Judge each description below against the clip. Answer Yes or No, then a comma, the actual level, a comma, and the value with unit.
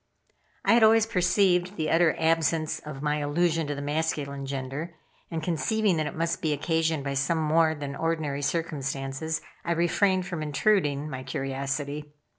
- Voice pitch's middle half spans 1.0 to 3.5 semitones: Yes, average, 2.9 semitones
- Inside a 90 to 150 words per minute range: No, average, 160 wpm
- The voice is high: No, medium, 155 Hz